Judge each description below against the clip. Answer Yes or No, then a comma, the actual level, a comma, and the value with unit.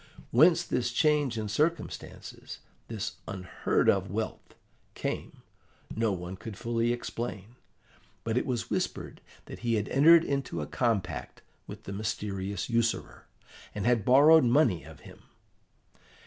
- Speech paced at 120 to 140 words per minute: Yes, slow, 135 wpm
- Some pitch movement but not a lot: Yes, average, 3.9 semitones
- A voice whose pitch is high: No, low, 115 Hz